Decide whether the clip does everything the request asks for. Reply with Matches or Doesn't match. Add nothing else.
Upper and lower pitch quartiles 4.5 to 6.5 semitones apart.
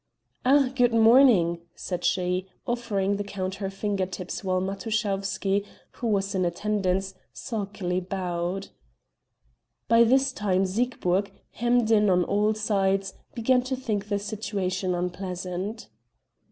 Doesn't match